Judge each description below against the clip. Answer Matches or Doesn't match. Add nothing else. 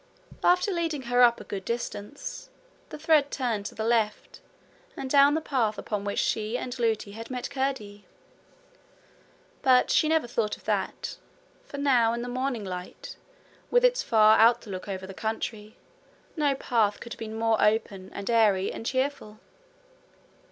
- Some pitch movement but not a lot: Matches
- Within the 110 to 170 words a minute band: Matches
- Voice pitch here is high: Matches